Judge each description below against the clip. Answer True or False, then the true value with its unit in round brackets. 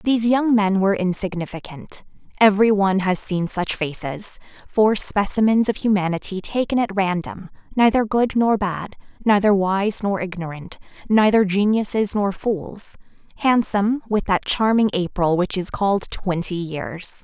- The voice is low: False (200 Hz)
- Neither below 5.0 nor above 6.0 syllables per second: False (4.7 syllables/s)